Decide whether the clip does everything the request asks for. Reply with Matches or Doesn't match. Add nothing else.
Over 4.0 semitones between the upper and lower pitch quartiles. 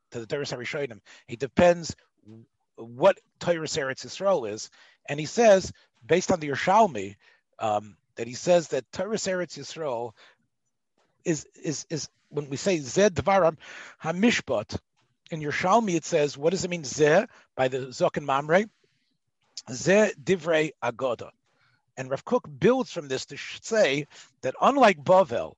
Matches